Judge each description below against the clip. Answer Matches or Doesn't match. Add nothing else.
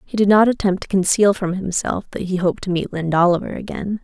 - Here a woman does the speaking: Matches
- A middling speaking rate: Doesn't match